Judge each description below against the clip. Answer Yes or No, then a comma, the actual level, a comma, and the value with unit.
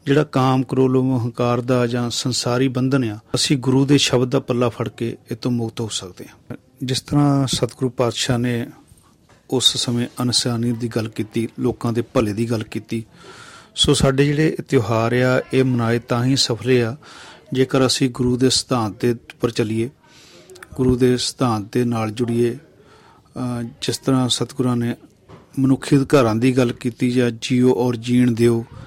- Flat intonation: Yes, narrow, 1.7 semitones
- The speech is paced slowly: No, fast, 165 wpm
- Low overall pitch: Yes, low, 125 Hz